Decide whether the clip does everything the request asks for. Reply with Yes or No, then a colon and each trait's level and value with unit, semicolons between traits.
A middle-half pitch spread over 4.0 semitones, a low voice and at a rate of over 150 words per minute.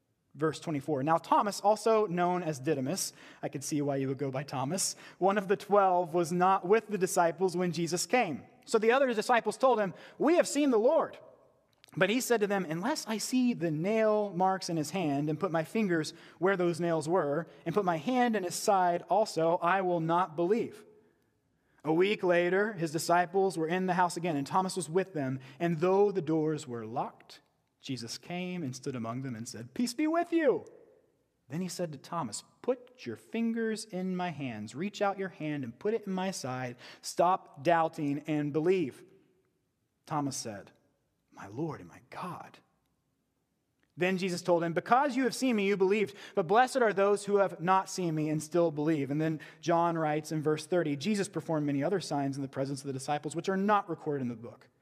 No: average, 4.6 semitones; medium, 175 Hz; fast, 205 wpm